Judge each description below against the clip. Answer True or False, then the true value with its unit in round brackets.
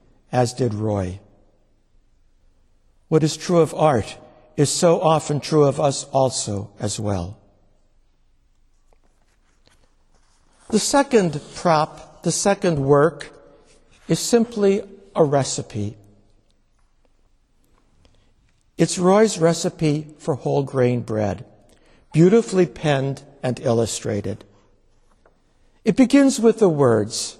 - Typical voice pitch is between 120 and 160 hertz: True (140 Hz)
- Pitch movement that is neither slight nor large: False (8.0 semitones)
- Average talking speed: False (95 wpm)